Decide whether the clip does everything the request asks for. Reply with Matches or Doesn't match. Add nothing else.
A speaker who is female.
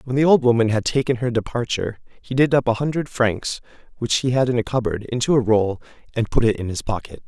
Doesn't match